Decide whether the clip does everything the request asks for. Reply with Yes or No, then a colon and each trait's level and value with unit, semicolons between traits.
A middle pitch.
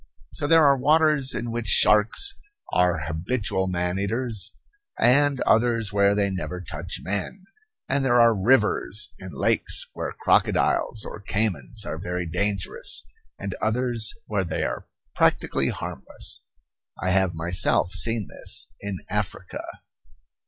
No: low, 105 Hz